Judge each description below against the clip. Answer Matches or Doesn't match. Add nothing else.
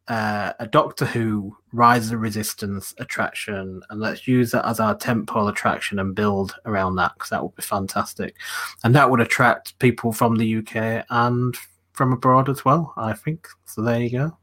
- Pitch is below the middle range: Matches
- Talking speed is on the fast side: Doesn't match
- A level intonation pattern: Doesn't match